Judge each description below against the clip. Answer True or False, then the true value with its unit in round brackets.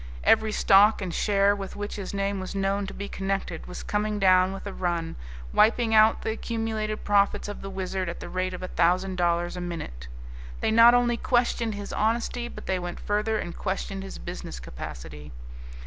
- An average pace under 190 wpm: False (195 wpm)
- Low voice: False (195 Hz)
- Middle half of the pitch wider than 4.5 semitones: False (2.9 semitones)